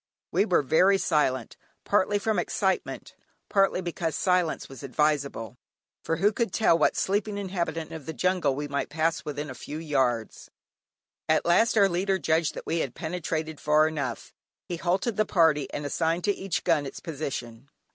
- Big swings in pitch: No, average, 4.3 semitones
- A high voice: No, medium, 165 Hz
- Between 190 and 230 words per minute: No, average, 170 wpm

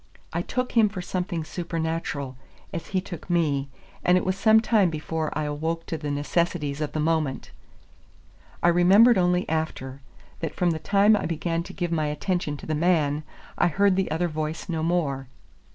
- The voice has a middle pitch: Yes, medium, 165 Hz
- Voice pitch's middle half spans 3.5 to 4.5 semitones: No, average, 2.9 semitones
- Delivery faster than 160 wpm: Yes, average, 185 wpm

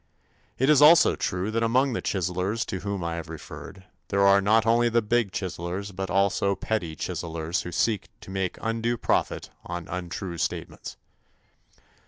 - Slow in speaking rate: No, average, 165 wpm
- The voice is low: Yes, low, 100 Hz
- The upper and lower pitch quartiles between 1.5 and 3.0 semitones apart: No, average, 4.2 semitones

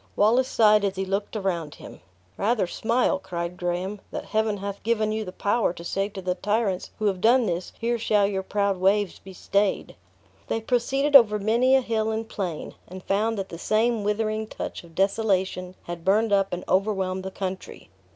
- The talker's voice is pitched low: No, high, 200 Hz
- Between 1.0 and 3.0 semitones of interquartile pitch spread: Yes, average, 2.7 semitones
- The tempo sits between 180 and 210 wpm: Yes, average, 190 wpm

